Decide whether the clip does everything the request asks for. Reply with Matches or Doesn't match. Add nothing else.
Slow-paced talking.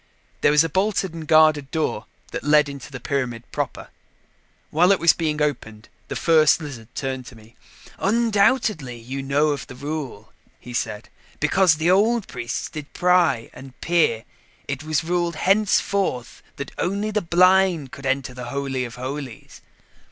Doesn't match